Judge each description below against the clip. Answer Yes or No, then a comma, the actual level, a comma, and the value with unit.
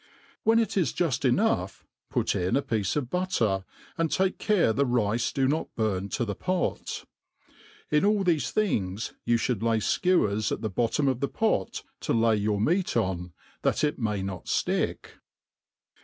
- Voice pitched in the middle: No, low, 120 Hz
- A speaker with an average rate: Yes, average, 170 wpm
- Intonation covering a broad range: Yes, wide, 8.2 semitones